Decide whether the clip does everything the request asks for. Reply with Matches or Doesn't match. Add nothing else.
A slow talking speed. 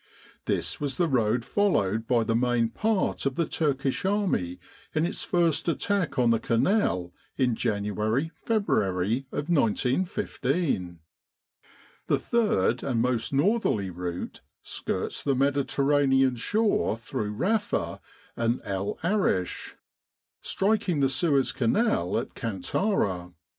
Matches